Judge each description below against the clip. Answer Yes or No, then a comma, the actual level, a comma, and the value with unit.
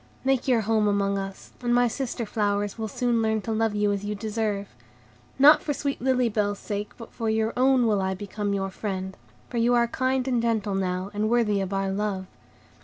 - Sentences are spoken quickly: Yes, fast, 210 wpm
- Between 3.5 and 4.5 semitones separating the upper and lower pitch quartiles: No, average, 3.0 semitones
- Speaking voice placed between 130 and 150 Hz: No, high, 215 Hz